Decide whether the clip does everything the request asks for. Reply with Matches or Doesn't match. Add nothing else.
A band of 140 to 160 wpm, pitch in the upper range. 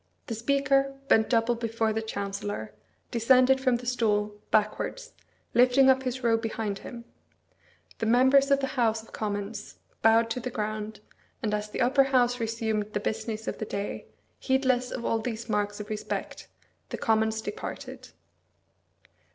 Matches